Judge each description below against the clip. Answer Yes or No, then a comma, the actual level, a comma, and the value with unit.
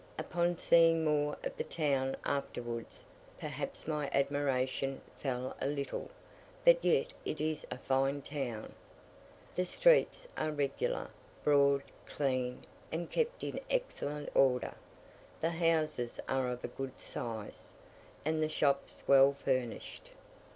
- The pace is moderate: No, slow, 125 wpm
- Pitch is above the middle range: No, medium, 140 Hz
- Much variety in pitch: No, average, 3.3 semitones